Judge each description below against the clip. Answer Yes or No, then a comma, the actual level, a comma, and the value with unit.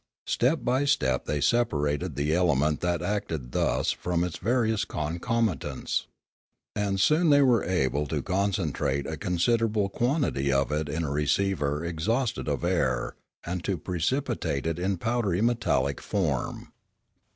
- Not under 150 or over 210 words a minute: No, average, 140 wpm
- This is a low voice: Yes, very low, 90 Hz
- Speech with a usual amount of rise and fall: No, wide, 7.3 semitones